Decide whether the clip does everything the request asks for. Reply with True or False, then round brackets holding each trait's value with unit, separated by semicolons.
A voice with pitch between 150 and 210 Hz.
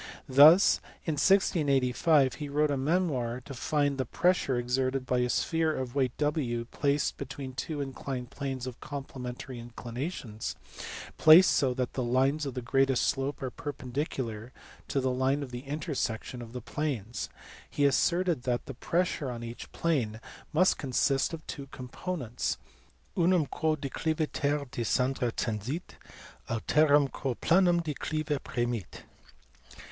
False (135 Hz)